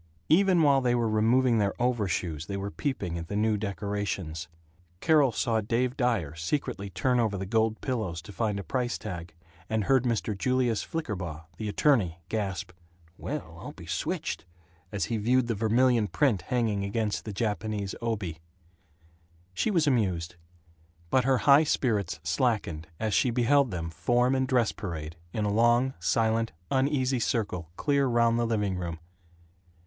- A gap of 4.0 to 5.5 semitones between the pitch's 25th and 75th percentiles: Yes, average, 4.3 semitones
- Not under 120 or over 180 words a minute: Yes, average, 160 wpm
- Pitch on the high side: No, low, 110 Hz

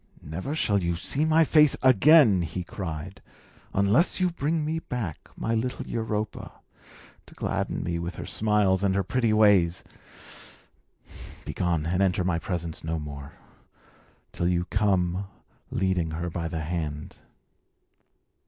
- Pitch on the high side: No, very low, 95 Hz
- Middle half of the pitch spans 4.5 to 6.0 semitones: Yes, average, 4.8 semitones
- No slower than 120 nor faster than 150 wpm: Yes, slow, 135 wpm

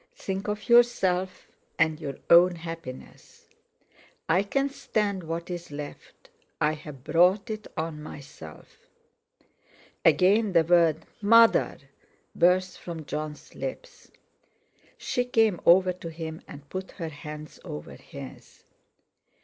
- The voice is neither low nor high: Yes, medium, 170 Hz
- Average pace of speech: No, slow, 110 wpm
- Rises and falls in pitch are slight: No, average, 3.9 semitones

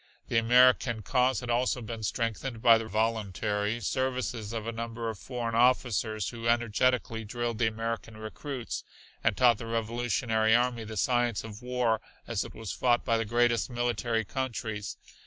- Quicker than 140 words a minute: Yes, average, 160 wpm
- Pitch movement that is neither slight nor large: No, narrow, 1.6 semitones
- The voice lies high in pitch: No, low, 115 Hz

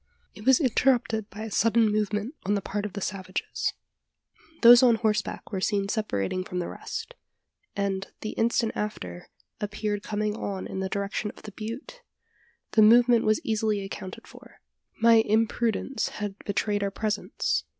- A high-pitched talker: Yes, high, 210 Hz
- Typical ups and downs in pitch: No, narrow, 2.1 semitones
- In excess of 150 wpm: Yes, average, 160 wpm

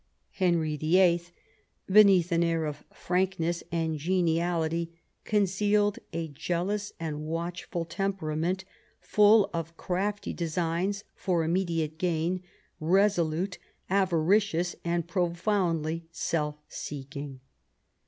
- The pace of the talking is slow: Yes, slow, 95 wpm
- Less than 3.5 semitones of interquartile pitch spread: Yes, average, 2.7 semitones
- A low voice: No, medium, 170 Hz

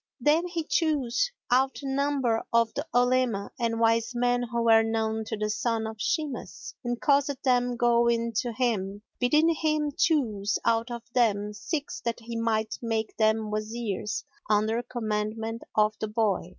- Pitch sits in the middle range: No, high, 235 Hz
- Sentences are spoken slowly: No, average, 165 wpm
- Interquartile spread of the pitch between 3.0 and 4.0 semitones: No, narrow, 2.6 semitones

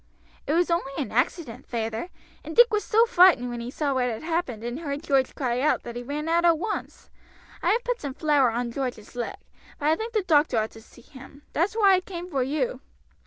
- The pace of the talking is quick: Yes, fast, 230 wpm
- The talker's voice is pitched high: Yes, very high, 290 Hz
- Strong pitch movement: Yes, wide, 5.9 semitones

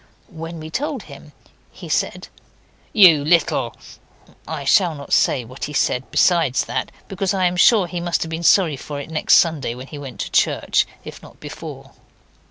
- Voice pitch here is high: No, medium, 160 Hz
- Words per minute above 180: Yes, average, 190 wpm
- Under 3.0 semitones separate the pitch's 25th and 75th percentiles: No, average, 3.8 semitones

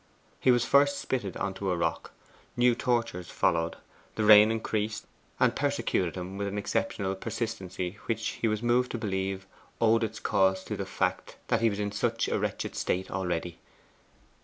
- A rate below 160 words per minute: No, average, 175 wpm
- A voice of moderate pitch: No, low, 105 Hz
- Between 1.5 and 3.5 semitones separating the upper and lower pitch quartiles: Yes, average, 3.2 semitones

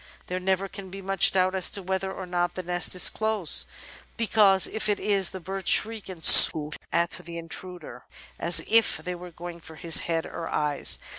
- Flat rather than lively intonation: Yes, narrow, 2.3 semitones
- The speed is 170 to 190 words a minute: No, average, 200 wpm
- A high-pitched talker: No, medium, 180 Hz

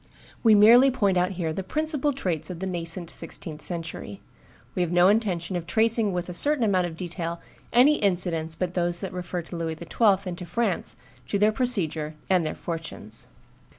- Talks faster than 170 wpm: Yes, average, 185 wpm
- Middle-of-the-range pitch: Yes, medium, 180 Hz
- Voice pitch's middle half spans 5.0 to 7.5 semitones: No, average, 4.0 semitones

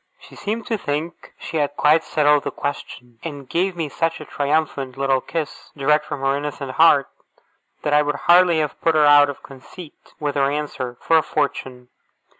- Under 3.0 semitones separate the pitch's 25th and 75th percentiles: Yes, narrow, 2.4 semitones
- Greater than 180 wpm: Yes, average, 190 wpm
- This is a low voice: No, medium, 150 Hz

